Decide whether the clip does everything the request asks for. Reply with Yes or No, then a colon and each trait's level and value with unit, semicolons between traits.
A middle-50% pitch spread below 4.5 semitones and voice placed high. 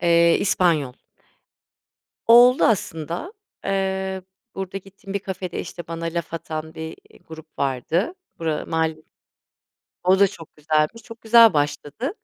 No: average, 3.6 semitones; medium, 170 Hz